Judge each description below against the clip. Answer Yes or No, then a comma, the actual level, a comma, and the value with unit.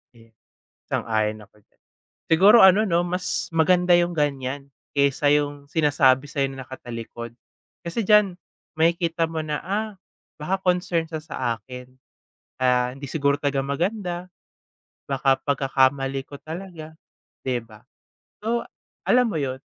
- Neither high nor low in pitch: Yes, medium, 150 Hz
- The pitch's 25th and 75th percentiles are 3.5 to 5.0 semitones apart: Yes, average, 4.7 semitones